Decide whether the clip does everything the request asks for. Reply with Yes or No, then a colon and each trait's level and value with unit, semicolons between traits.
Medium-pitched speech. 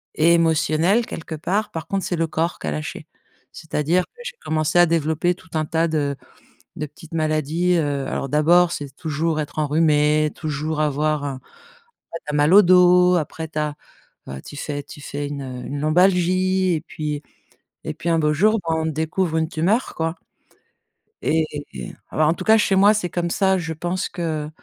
Yes: medium, 160 Hz